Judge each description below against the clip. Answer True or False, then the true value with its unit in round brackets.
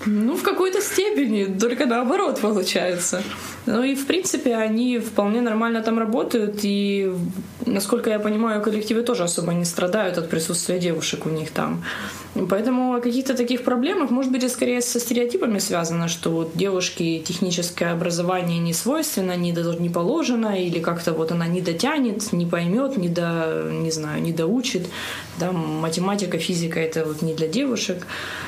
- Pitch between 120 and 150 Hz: False (195 Hz)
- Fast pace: True (160 wpm)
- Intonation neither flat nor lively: False (5.9 semitones)